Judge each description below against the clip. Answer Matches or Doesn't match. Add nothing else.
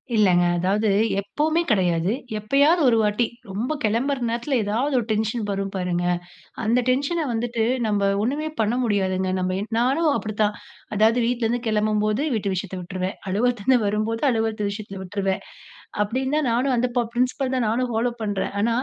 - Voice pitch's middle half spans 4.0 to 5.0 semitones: Doesn't match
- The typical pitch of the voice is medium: Doesn't match